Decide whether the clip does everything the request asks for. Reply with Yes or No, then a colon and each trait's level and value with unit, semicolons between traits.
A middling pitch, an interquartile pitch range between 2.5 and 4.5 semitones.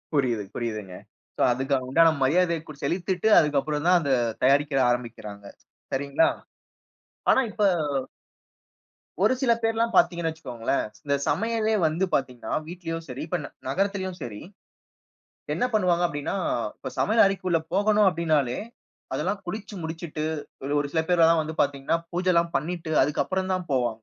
No: medium, 165 Hz; average, 5.0 semitones